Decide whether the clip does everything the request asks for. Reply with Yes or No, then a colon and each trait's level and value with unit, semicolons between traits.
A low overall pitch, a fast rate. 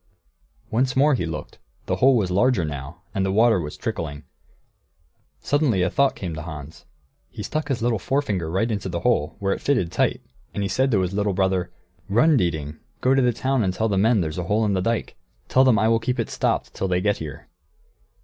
Yes: low, 100 Hz; fast, 220 wpm